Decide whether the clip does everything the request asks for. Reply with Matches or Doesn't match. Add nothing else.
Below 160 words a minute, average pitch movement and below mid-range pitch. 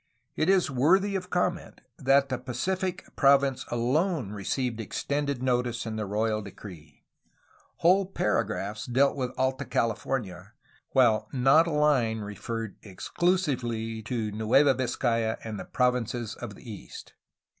Matches